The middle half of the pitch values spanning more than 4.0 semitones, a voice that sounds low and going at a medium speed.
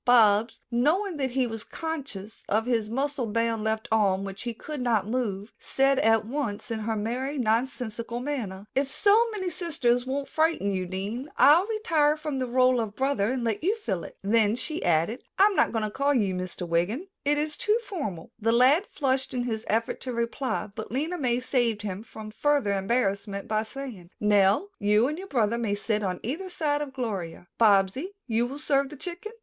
No: average, 5.1 semitones; high, 240 Hz; average, 195 wpm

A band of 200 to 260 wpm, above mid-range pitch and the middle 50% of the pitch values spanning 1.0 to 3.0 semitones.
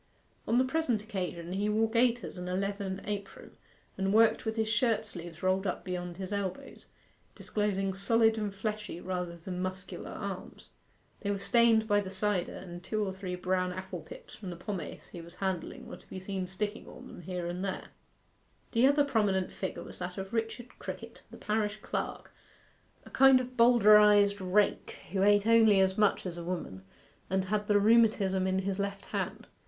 No: average, 185 wpm; high, 200 Hz; average, 2.7 semitones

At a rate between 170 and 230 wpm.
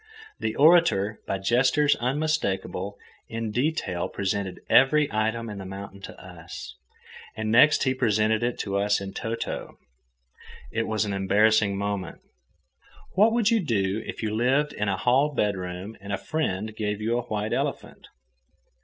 No: average, 155 wpm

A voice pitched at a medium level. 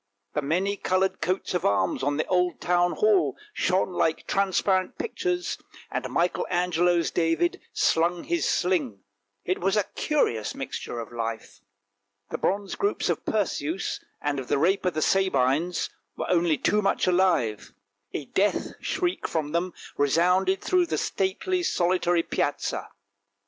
Yes: medium, 180 Hz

